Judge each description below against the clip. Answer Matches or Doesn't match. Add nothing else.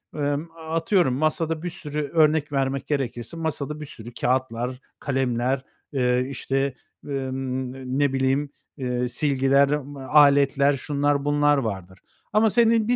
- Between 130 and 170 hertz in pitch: Matches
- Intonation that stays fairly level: Matches